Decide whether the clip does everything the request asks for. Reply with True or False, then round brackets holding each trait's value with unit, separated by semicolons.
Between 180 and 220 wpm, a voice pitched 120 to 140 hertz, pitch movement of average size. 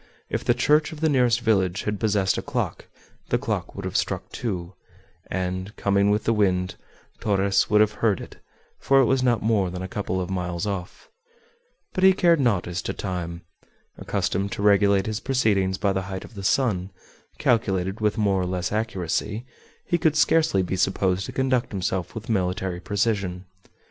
False (185 wpm; 100 Hz; 3.5 semitones)